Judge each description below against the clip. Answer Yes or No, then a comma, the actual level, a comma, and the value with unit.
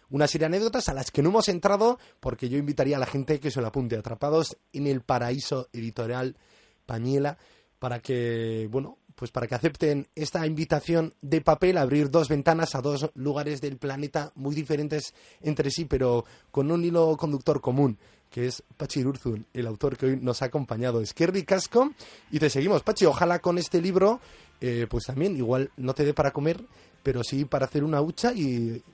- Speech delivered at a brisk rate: Yes, fast, 195 wpm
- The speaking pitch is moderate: Yes, medium, 145 Hz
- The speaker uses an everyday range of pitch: Yes, average, 4.1 semitones